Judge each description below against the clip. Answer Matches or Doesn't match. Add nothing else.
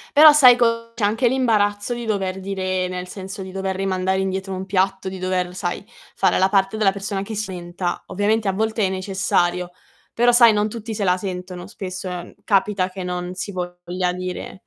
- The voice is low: Doesn't match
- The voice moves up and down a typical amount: Doesn't match